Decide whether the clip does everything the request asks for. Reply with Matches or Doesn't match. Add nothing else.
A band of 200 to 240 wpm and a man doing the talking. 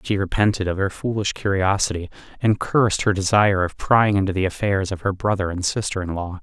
Matches